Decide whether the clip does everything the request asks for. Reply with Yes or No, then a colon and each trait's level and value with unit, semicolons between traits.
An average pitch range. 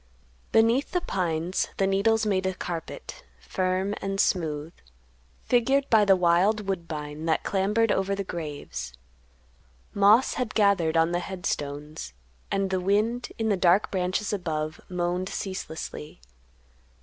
Yes: average, 3.7 semitones